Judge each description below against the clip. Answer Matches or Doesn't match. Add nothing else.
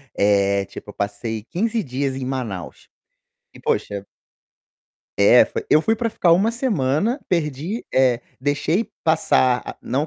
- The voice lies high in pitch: Doesn't match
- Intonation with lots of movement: Matches